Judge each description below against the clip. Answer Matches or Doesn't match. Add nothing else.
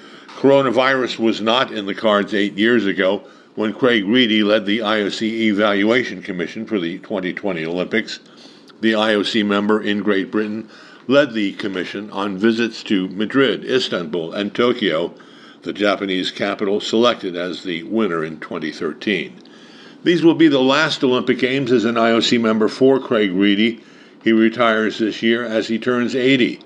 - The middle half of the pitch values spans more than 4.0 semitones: Doesn't match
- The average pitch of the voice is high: Doesn't match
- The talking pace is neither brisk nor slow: Matches